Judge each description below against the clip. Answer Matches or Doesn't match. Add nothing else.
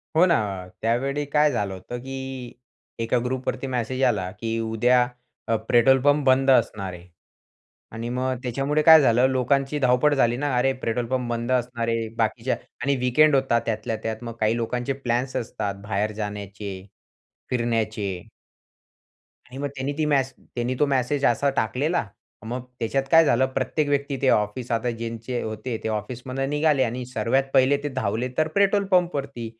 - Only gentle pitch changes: Doesn't match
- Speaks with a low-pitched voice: Matches